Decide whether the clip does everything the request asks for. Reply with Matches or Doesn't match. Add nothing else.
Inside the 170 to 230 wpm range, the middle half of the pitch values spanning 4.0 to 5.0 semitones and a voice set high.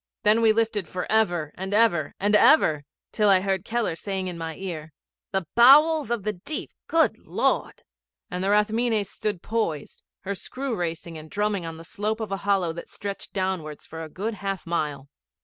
Matches